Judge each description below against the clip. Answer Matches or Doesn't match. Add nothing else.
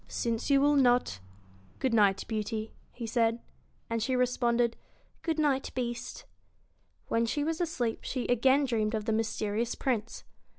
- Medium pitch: Doesn't match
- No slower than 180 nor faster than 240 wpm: Doesn't match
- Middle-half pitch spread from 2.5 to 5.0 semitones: Matches